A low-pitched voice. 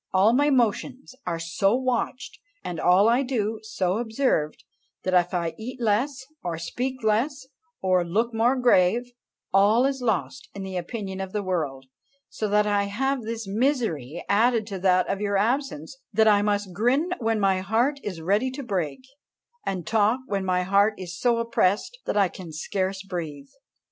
No: high, 205 Hz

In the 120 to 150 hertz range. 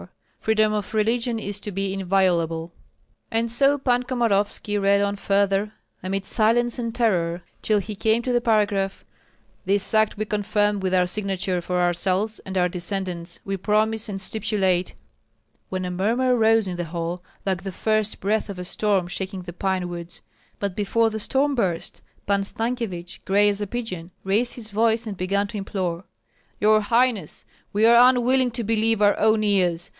No: high, 205 Hz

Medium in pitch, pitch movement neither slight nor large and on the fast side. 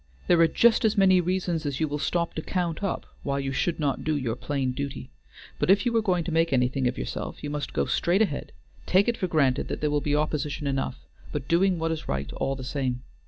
Yes: medium, 150 Hz; average, 4.4 semitones; fast, 245 wpm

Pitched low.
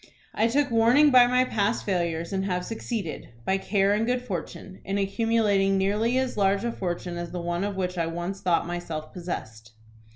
No: high, 195 Hz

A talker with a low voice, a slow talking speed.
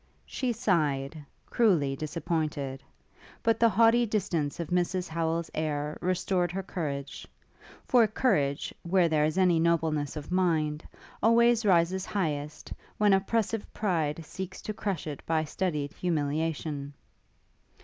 No: medium, 170 Hz; slow, 125 wpm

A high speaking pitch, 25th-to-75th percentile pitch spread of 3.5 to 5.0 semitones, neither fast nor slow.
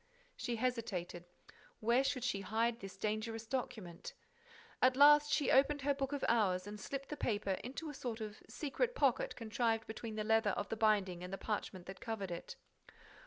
Yes: high, 225 Hz; average, 4.3 semitones; average, 180 wpm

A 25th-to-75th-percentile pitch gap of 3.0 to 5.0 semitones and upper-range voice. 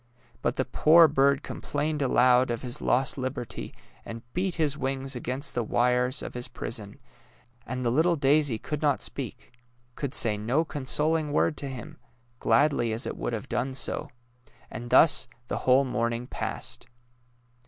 No: average, 3.4 semitones; low, 130 Hz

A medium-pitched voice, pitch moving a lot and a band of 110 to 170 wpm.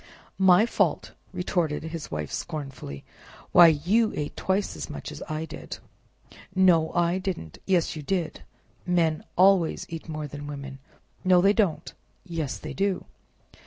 No: medium, 165 Hz; average, 3.6 semitones; average, 145 wpm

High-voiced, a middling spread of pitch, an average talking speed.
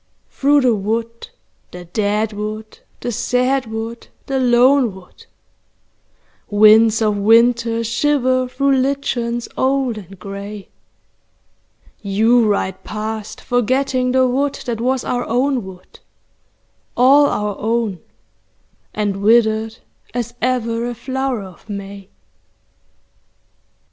No: high, 230 Hz; average, 3.2 semitones; slow, 110 wpm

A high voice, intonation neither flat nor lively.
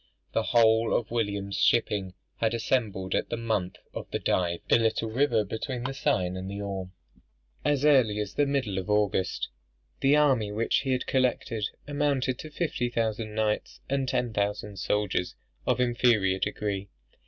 No: low, 110 Hz; average, 3.9 semitones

